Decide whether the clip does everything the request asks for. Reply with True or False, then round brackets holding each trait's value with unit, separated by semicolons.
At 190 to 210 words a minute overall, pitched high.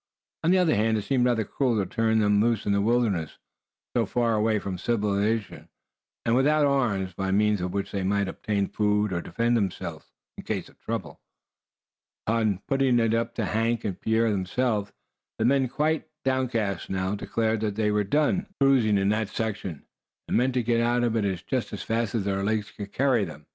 False (195 wpm; 110 Hz)